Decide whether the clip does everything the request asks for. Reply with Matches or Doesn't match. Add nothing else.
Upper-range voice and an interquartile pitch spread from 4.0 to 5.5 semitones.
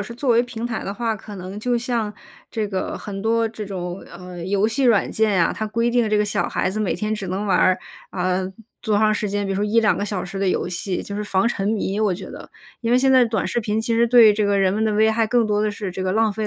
Doesn't match